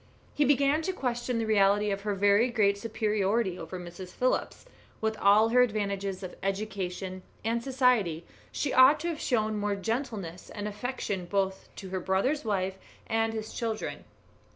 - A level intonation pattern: No, average, 3.5 semitones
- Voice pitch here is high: Yes, high, 210 Hz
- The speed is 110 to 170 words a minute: Yes, average, 160 wpm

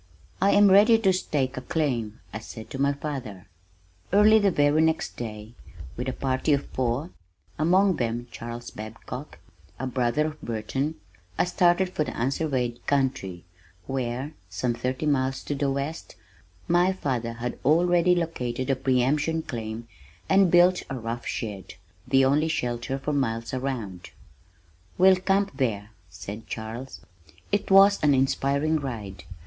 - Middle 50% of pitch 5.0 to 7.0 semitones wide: Yes, average, 5.3 semitones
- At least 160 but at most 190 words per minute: No, average, 150 wpm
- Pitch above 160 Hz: No, low, 135 Hz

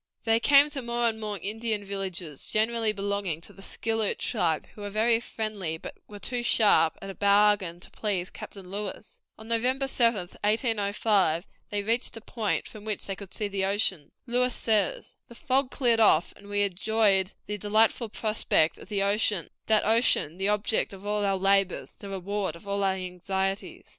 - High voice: Yes, high, 205 Hz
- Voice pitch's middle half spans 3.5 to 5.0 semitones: No, narrow, 2.5 semitones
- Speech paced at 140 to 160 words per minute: No, average, 185 wpm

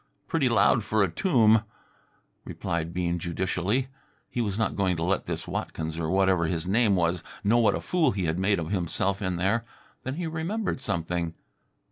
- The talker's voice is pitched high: No, very low, 95 Hz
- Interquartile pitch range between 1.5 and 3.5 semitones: No, average, 5.0 semitones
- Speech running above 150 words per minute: Yes, average, 180 wpm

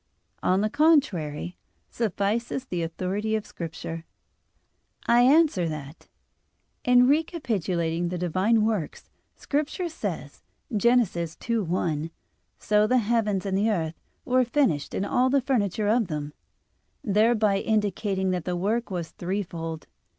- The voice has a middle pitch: No, high, 205 Hz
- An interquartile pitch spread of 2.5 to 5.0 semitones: No, wide, 5.4 semitones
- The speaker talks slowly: Yes, slow, 120 wpm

